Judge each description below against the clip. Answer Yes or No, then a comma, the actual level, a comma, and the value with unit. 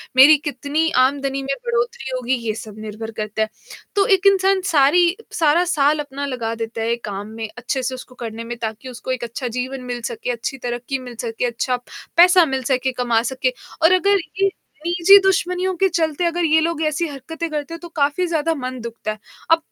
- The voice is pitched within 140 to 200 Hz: No, very high, 275 Hz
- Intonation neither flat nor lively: No, wide, 5.7 semitones